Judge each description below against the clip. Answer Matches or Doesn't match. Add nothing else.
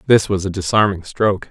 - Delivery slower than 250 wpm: Matches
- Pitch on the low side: Matches